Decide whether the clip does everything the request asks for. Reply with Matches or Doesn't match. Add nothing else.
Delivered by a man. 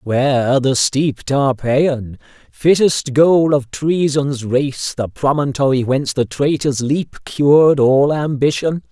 Matches